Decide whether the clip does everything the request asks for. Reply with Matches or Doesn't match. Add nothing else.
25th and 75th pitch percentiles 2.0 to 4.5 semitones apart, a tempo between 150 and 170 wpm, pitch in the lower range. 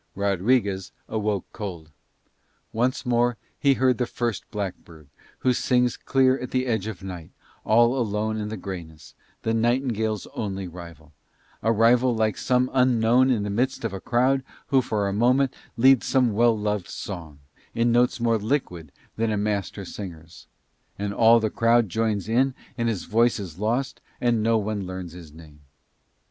Matches